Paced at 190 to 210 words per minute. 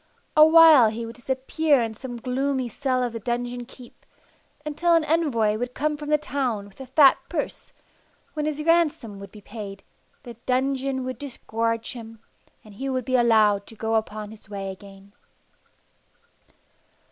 No: average, 165 wpm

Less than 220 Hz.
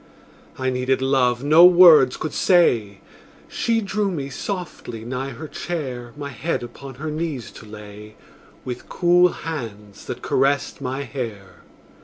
Yes: low, 135 Hz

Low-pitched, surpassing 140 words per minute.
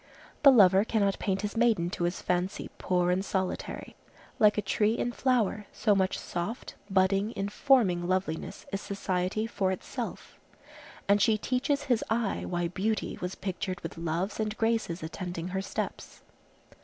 No: high, 195 Hz; average, 155 wpm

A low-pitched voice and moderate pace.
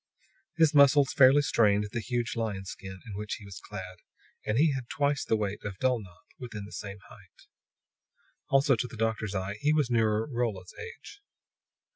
Yes: low, 115 Hz; average, 175 wpm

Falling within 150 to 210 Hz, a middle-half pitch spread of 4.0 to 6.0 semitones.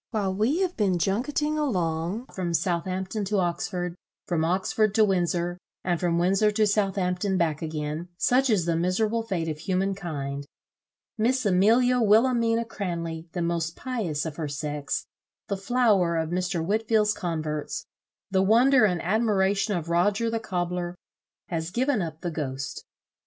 Yes: medium, 185 Hz; average, 4.3 semitones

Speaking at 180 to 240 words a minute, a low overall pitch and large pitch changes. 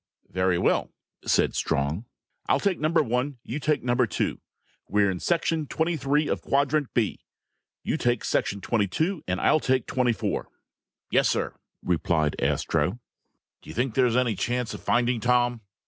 No: average, 165 wpm; low, 125 Hz; wide, 5.9 semitones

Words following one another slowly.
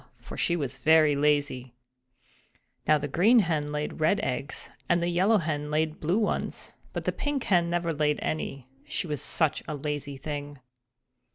No: average, 170 wpm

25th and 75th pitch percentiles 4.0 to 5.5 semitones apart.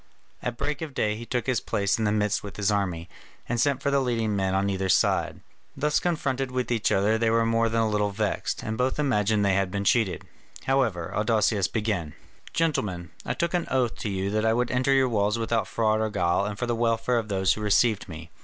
No: average, 3.5 semitones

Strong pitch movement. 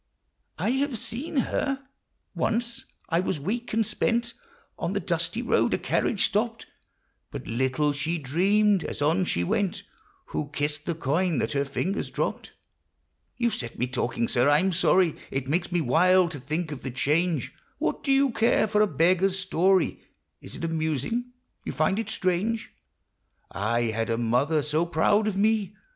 Yes: wide, 6.6 semitones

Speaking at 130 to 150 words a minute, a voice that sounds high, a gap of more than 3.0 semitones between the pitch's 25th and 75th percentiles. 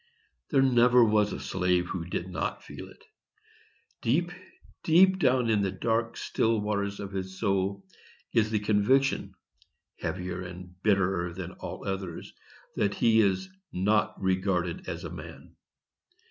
No: slow, 135 wpm; low, 100 Hz; average, 3.5 semitones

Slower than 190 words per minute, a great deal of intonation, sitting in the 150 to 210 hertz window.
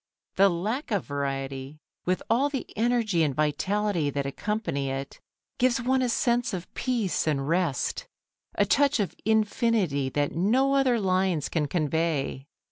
Yes: average, 145 wpm; wide, 8.1 semitones; medium, 185 Hz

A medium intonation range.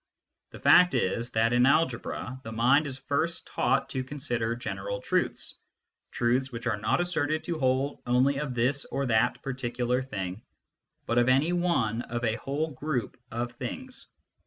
Yes: average, 3.2 semitones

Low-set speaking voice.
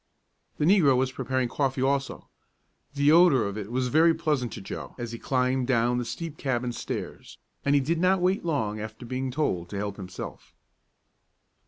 Yes: low, 130 Hz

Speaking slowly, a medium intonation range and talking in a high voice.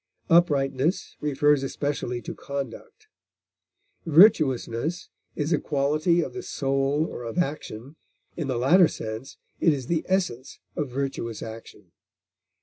No: slow, 125 wpm; average, 3.9 semitones; medium, 140 Hz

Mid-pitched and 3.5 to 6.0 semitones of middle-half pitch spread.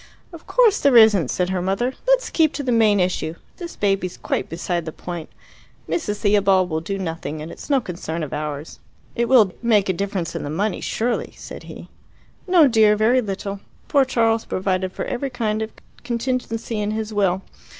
No: high, 205 Hz; average, 4.6 semitones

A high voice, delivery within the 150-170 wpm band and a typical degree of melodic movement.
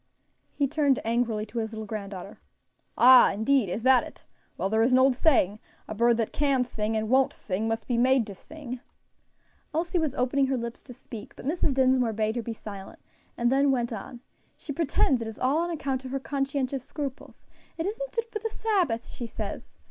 No: very high, 255 Hz; average, 200 wpm; average, 3.7 semitones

